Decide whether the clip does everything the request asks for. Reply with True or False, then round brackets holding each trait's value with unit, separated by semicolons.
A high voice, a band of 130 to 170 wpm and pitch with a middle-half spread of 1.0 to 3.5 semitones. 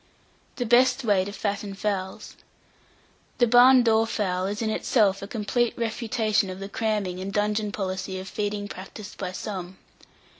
True (205 Hz; 155 wpm; 2.6 semitones)